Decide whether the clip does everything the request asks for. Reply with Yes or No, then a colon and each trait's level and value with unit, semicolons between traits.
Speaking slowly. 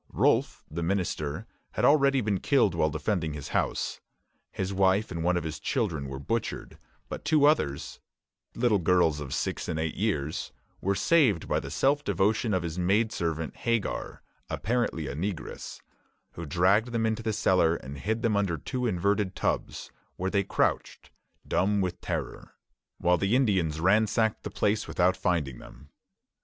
No: average, 165 wpm